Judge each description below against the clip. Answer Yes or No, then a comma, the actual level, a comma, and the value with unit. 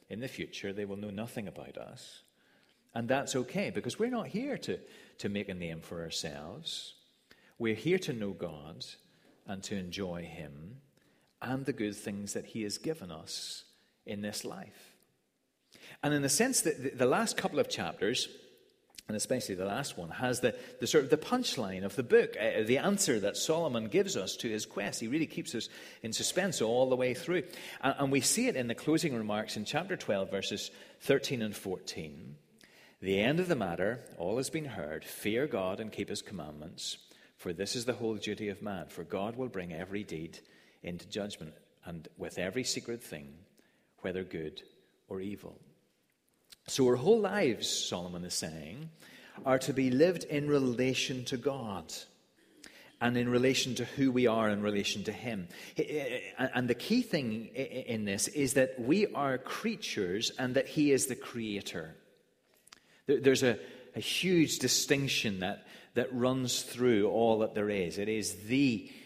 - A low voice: Yes, low, 125 Hz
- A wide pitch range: Yes, wide, 5.9 semitones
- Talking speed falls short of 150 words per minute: No, average, 175 wpm